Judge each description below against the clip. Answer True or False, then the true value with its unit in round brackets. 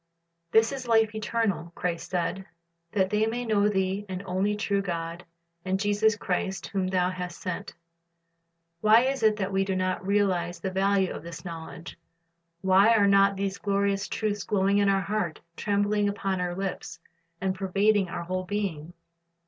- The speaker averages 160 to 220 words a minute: True (170 wpm)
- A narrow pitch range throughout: True (1.9 semitones)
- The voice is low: False (195 Hz)